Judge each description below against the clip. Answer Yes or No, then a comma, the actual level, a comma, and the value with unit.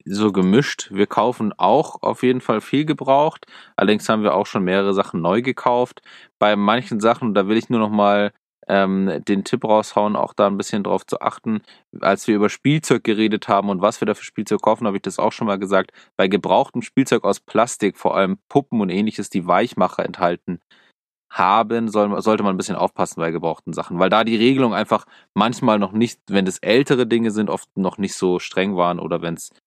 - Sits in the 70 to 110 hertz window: Yes, low, 105 Hz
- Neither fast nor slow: No, fast, 210 wpm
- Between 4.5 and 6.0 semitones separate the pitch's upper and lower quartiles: No, average, 3.1 semitones